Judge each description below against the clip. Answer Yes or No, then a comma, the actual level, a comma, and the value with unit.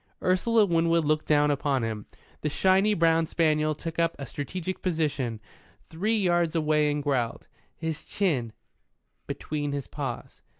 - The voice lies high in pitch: No, medium, 155 Hz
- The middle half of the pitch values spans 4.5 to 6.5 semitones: No, average, 2.9 semitones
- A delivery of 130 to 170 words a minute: Yes, average, 140 wpm